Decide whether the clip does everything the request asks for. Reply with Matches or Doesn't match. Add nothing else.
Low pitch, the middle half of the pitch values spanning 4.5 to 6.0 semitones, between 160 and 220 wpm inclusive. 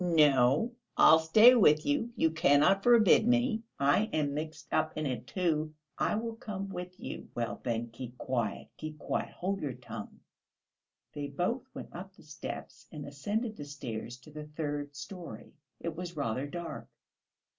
Doesn't match